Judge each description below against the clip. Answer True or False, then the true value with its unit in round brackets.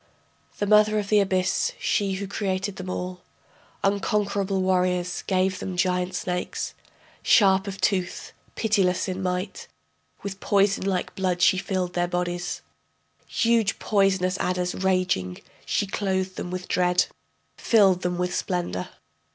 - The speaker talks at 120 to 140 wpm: True (135 wpm)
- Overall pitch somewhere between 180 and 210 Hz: True (185 Hz)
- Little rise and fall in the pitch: True (1.6 semitones)